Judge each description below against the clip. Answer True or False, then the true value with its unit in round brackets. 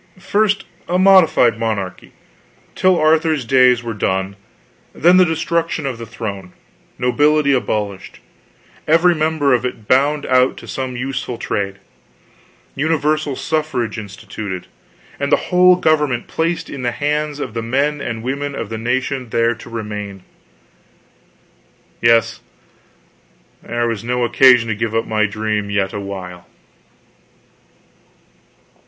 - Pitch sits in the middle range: False (125 Hz)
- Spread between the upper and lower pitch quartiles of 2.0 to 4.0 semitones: False (5.5 semitones)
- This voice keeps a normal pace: False (130 wpm)